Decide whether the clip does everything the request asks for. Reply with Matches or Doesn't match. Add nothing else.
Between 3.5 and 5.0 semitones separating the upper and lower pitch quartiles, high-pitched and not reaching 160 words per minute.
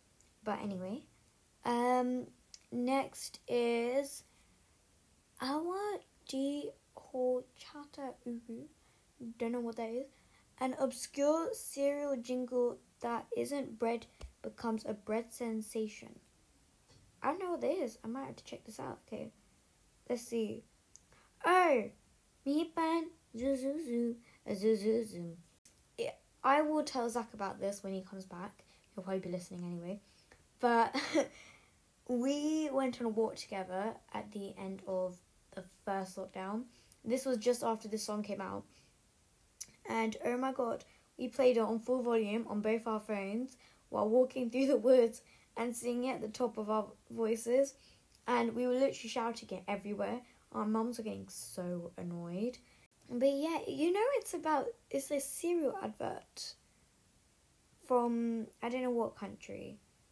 Matches